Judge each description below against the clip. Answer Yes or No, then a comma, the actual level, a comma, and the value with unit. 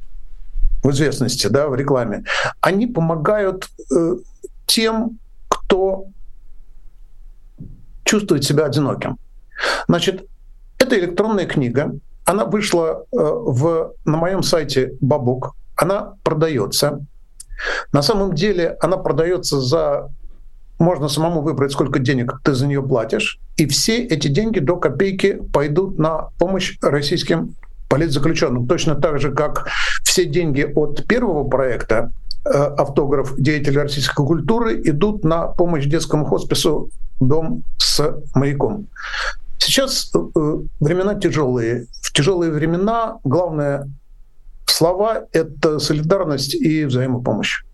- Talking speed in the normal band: No, slow, 105 wpm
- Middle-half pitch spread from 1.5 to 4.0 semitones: No, average, 4.5 semitones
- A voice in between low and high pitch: Yes, medium, 155 Hz